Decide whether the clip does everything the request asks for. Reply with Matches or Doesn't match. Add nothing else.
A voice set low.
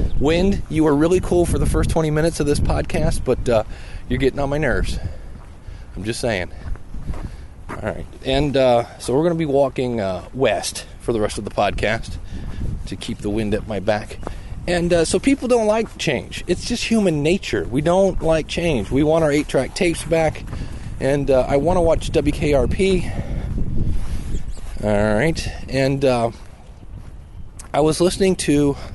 Matches